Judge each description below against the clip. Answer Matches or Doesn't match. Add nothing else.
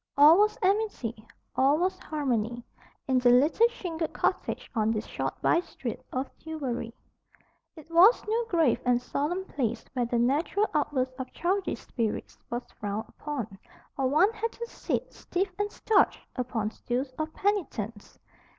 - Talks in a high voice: Matches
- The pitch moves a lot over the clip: Matches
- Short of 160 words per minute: Matches